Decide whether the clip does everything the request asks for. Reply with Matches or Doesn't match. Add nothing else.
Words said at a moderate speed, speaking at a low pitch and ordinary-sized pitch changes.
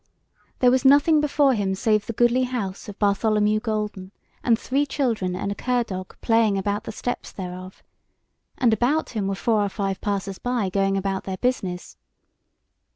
Doesn't match